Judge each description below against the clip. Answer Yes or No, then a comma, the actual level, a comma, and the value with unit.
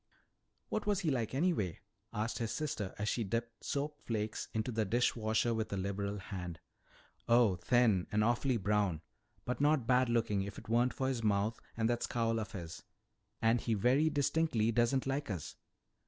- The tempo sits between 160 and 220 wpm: Yes, average, 180 wpm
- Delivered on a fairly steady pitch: No, average, 3.3 semitones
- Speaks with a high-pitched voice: No, low, 115 Hz